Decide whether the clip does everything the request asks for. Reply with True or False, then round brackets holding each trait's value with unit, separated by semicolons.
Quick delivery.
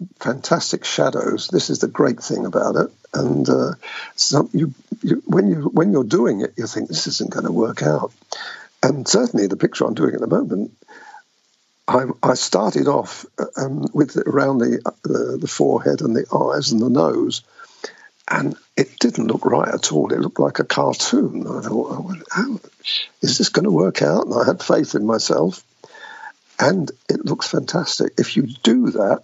False (185 wpm)